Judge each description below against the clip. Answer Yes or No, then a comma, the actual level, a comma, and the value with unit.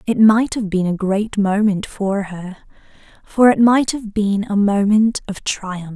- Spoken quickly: No, average, 180 wpm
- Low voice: No, high, 205 Hz